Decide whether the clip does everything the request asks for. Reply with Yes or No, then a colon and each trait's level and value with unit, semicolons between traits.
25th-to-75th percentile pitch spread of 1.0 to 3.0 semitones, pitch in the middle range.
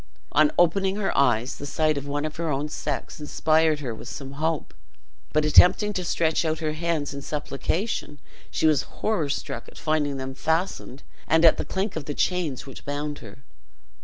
Yes: narrow, 2.5 semitones; medium, 155 Hz